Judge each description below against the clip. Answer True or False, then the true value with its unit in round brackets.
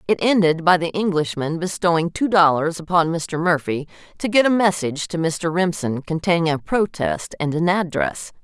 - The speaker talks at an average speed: True (170 wpm)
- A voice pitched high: False (165 Hz)